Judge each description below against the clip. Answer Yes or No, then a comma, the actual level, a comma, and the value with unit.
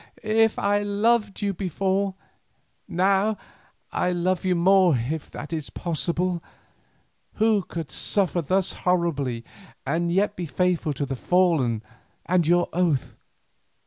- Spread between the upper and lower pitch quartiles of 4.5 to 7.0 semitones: No, average, 3.2 semitones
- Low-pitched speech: No, medium, 180 Hz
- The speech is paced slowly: Yes, slow, 125 wpm